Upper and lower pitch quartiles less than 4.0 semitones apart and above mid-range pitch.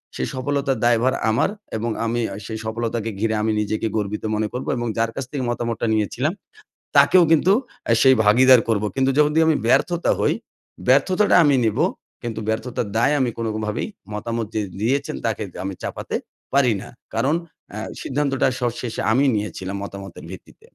No: average, 3.6 semitones; low, 115 Hz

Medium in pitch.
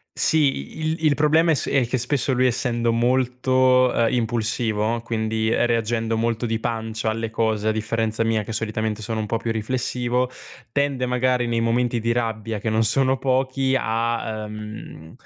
No: low, 115 Hz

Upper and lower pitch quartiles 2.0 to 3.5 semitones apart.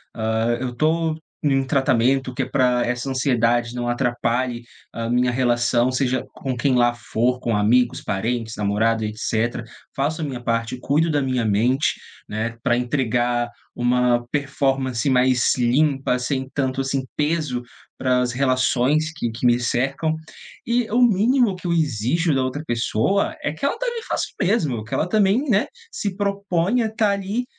No: average, 4.4 semitones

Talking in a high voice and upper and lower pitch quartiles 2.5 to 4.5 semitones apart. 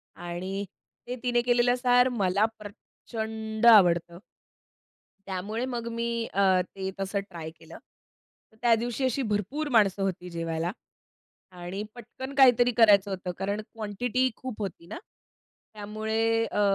Yes: high, 215 Hz; average, 4.0 semitones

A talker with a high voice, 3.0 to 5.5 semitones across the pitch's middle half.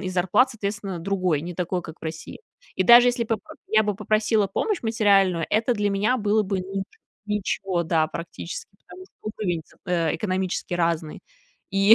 Yes: high, 195 Hz; average, 3.4 semitones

